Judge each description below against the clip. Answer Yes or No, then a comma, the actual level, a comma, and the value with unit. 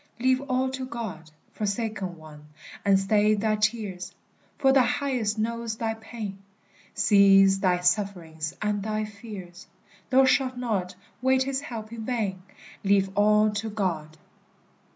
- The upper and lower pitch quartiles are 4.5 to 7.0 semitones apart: No, average, 3.3 semitones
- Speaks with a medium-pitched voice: No, high, 210 Hz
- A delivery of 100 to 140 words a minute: Yes, slow, 135 wpm